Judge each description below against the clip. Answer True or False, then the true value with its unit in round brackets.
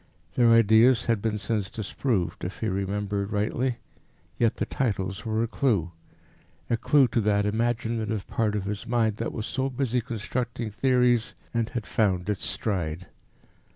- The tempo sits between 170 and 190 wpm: False (155 wpm)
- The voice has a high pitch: False (110 Hz)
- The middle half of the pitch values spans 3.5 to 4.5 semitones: False (2.6 semitones)